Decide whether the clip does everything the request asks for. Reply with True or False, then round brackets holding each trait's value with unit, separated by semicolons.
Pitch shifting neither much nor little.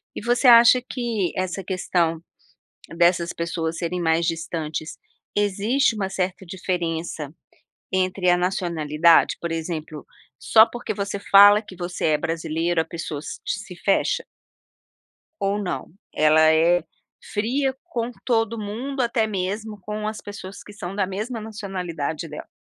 True (4.3 semitones)